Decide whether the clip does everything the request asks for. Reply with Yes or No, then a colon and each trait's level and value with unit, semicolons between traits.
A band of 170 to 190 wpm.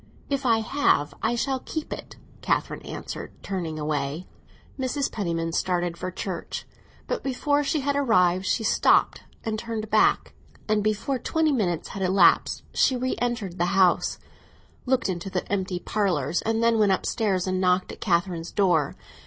No: average, 160 wpm